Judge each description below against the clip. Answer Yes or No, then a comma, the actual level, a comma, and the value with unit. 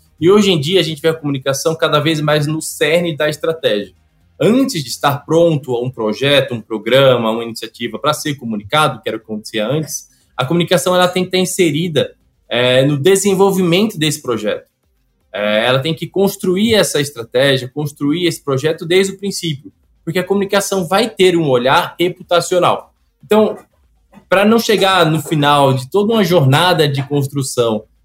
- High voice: No, medium, 155 Hz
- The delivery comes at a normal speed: Yes, average, 170 wpm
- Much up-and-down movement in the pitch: Yes, wide, 6.1 semitones